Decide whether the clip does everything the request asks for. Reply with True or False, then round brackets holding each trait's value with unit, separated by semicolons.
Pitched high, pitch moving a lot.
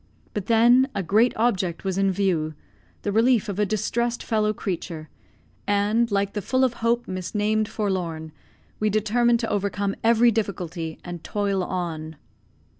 False (205 Hz; 3.5 semitones)